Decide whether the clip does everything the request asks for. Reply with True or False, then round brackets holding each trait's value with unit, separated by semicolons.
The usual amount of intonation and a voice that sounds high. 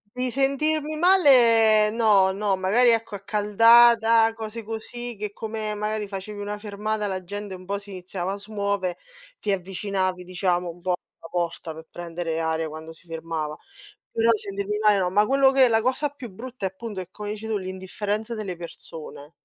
True (3.4 semitones; 205 Hz)